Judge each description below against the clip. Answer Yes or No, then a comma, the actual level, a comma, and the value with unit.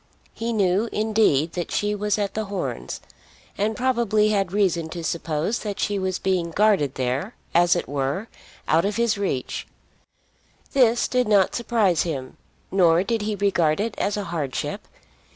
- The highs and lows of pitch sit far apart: No, average, 4.2 semitones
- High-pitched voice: Yes, high, 200 Hz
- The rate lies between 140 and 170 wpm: Yes, average, 160 wpm